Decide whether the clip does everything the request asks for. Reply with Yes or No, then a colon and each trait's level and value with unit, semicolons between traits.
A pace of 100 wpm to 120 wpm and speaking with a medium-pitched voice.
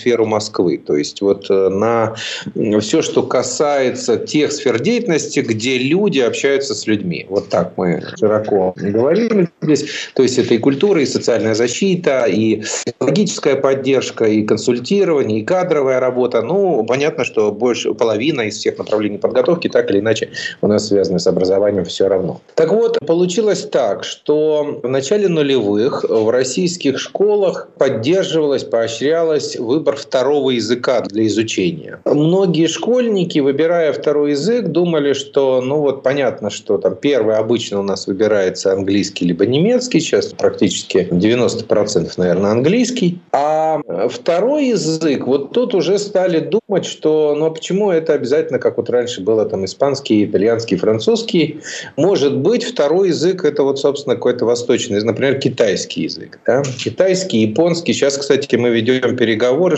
No: average, 145 wpm; medium, 160 Hz